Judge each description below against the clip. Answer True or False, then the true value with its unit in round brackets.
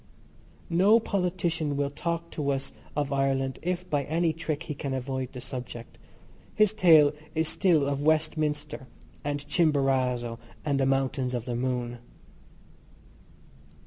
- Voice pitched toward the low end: False (145 Hz)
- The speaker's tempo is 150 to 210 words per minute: False (135 wpm)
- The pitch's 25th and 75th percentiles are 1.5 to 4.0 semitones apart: True (3.5 semitones)